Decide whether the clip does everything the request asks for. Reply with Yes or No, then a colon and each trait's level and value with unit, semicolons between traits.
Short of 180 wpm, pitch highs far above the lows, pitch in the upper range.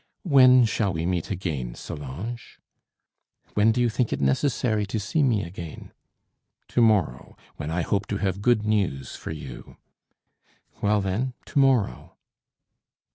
No: average, 140 wpm; wide, 6.0 semitones; low, 105 Hz